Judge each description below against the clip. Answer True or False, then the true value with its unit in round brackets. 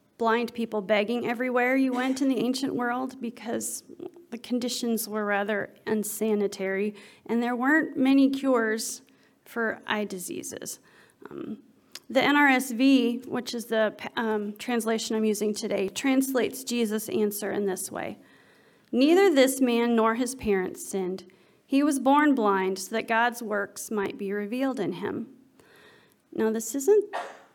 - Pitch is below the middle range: False (230 Hz)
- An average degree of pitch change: True (3.6 semitones)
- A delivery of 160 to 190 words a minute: False (140 wpm)